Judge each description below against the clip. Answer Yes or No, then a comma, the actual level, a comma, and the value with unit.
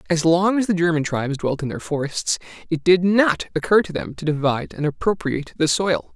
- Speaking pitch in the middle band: Yes, medium, 165 Hz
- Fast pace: Yes, fast, 215 wpm